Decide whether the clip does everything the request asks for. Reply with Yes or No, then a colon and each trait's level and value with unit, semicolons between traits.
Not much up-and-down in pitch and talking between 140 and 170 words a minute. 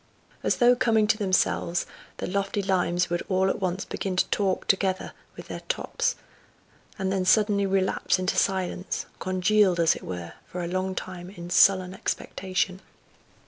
Yes: narrow, 1.4 semitones; average, 160 wpm